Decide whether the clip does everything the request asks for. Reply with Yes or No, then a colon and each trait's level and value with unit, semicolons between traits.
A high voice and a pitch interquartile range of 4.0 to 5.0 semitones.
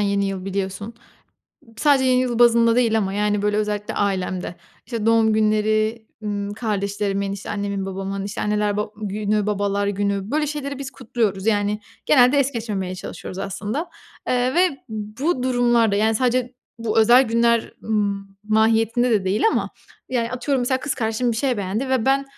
No: high, 215 Hz; average, 3.3 semitones